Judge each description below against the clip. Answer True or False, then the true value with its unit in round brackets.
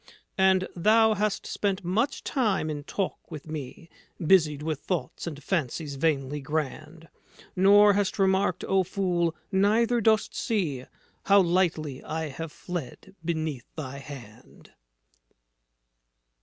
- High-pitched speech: False (170 Hz)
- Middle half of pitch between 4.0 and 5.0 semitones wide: True (4.6 semitones)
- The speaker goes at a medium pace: False (120 wpm)